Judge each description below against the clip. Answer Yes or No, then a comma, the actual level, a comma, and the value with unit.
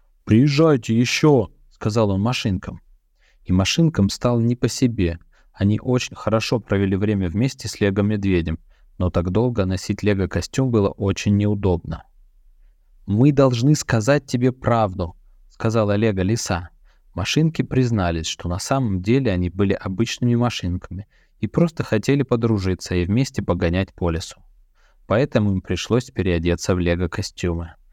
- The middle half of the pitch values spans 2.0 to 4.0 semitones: No, average, 5.2 semitones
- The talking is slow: No, average, 130 wpm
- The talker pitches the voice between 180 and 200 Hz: No, low, 105 Hz